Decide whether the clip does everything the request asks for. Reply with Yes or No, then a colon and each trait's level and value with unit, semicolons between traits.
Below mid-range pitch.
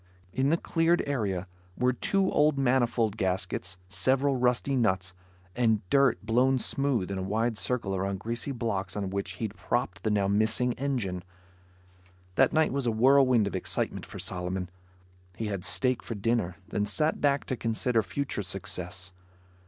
Yes: low, 115 Hz